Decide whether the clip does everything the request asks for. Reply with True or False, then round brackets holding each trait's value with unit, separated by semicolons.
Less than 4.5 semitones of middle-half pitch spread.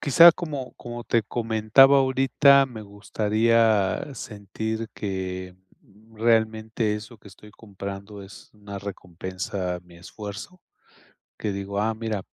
True (2.6 semitones)